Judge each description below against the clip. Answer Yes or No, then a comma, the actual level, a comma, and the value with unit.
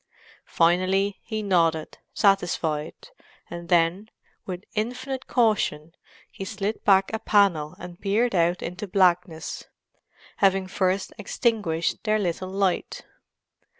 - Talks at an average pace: No, slow, 105 wpm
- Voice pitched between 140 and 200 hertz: Yes, high, 190 Hz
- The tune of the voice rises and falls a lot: No, average, 3.3 semitones